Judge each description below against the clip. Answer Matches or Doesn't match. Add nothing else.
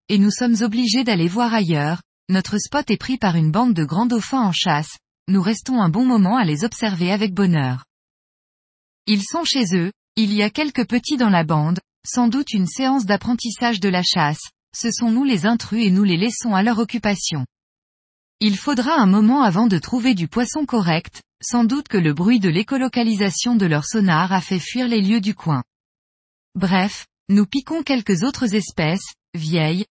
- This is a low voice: Doesn't match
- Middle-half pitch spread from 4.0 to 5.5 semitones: Matches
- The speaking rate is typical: Matches